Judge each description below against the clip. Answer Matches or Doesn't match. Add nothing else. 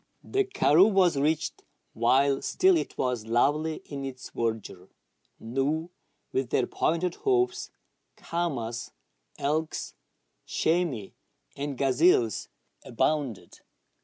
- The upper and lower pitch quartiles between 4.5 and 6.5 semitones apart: Matches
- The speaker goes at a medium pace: Doesn't match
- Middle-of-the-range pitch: Matches